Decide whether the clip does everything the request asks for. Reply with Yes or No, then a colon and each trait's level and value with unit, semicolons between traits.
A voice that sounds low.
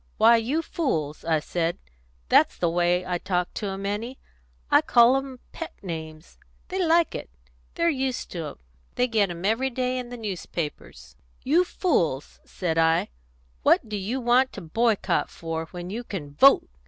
No: high, 205 Hz